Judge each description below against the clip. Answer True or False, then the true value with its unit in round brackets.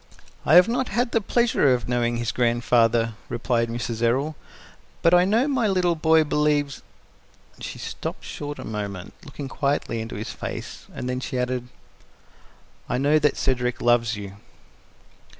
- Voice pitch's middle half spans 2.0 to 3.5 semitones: False (5.0 semitones)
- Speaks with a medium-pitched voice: False (125 Hz)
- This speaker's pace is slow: False (160 wpm)